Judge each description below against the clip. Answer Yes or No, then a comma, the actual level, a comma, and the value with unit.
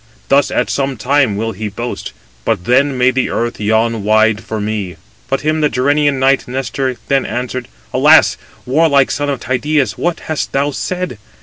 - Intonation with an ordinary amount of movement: Yes, average, 4.0 semitones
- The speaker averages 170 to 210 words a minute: Yes, average, 175 wpm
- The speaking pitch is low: Yes, low, 130 Hz